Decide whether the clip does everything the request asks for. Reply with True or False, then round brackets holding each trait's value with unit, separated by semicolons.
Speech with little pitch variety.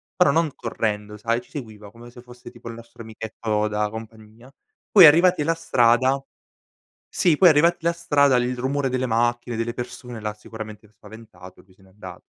False (4.0 semitones)